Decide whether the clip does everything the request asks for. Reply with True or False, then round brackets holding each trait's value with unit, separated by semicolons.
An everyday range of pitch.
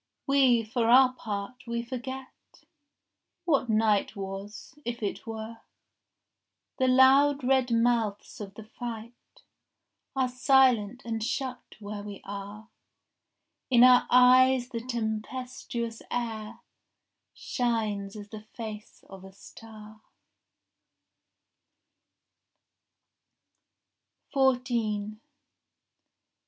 True (3.0 semitones)